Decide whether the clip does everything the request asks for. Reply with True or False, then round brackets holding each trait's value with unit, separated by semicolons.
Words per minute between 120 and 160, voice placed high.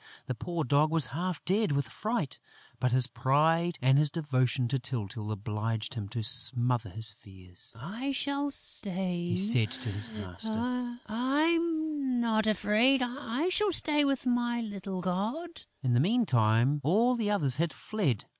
False (155 wpm; 175 Hz)